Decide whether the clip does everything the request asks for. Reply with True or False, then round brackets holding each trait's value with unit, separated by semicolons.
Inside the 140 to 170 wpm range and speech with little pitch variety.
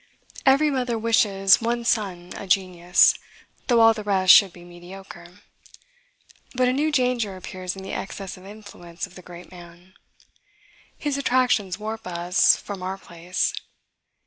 False (145 wpm; 4.1 semitones)